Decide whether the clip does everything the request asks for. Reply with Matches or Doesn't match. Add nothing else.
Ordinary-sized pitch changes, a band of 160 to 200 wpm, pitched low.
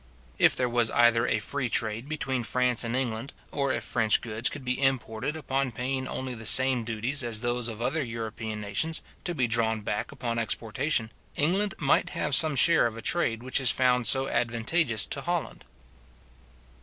Matches